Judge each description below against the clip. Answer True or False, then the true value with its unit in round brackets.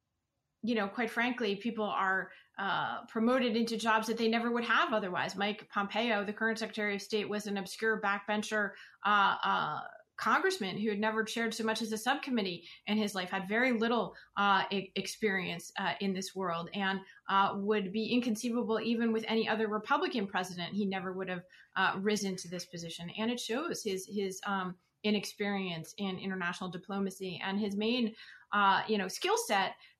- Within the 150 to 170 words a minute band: False (180 wpm)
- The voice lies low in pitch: False (205 Hz)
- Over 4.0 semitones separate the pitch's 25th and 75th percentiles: False (2.7 semitones)